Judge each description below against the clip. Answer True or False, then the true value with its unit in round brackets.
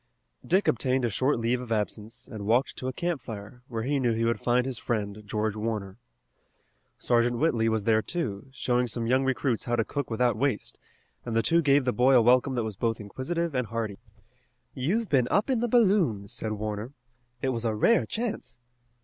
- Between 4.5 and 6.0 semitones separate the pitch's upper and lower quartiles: False (3.4 semitones)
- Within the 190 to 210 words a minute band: True (200 wpm)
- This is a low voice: True (120 Hz)